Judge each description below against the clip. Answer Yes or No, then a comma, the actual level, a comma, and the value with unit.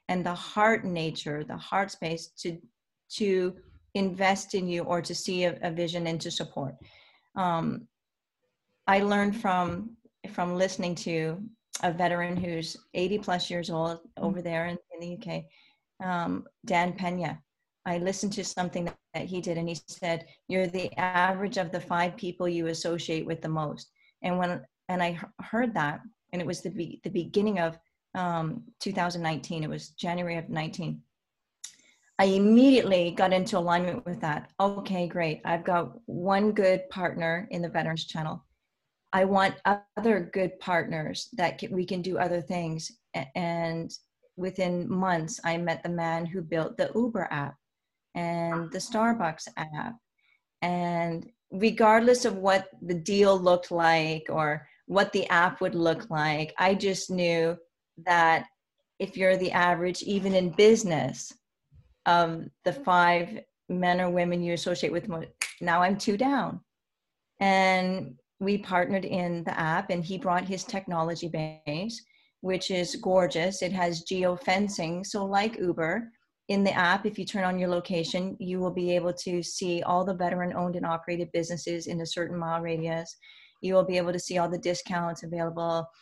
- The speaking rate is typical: Yes, average, 160 wpm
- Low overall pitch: No, medium, 180 Hz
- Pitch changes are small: Yes, narrow, 2.1 semitones